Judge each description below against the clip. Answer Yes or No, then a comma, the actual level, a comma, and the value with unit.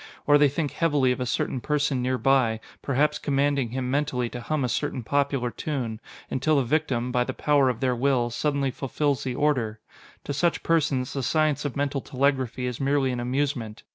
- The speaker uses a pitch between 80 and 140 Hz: Yes, low, 135 Hz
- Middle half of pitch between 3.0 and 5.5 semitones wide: No, narrow, 2.6 semitones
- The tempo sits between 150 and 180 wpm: No, average, 190 wpm